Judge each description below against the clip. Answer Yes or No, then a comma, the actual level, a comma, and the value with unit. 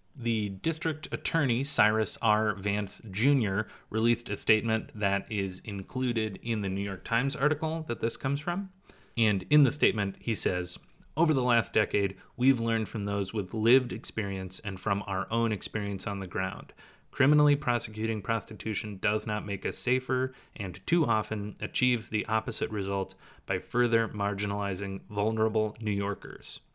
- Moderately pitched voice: No, low, 110 Hz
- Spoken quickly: No, average, 155 wpm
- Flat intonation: No, average, 3.2 semitones